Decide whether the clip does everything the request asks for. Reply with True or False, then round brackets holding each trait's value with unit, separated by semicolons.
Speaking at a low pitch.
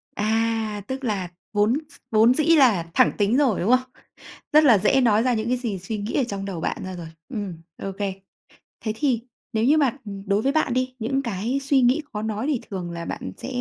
False (225 Hz)